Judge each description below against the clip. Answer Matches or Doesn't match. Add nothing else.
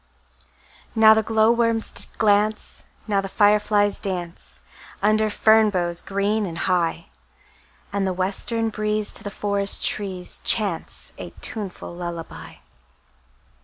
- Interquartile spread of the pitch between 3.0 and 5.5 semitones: Doesn't match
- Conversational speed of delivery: Doesn't match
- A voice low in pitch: Doesn't match